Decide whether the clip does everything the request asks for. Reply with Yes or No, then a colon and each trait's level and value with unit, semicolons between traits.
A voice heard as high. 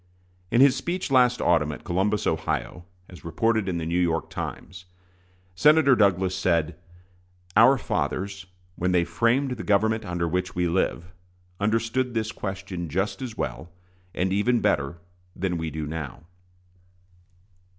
No: very low, 95 Hz